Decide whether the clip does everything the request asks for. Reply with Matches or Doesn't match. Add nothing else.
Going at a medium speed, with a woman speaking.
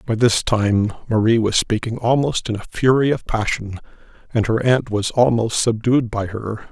Doesn't match